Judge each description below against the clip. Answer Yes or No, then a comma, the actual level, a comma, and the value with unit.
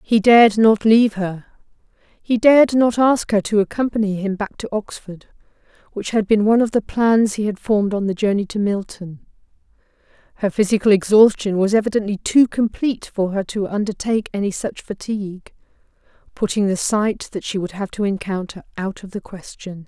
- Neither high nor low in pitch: No, high, 205 Hz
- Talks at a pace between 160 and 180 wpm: Yes, average, 170 wpm